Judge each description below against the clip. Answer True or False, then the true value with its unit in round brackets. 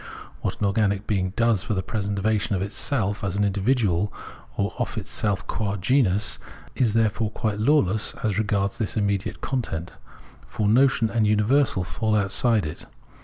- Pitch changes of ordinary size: False (2.2 semitones)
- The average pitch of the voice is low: True (105 Hz)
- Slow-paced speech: False (155 wpm)